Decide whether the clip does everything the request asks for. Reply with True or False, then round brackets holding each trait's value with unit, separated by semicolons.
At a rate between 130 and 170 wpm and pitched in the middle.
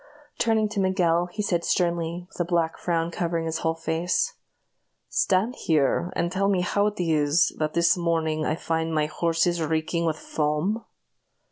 True (165 wpm; 170 Hz)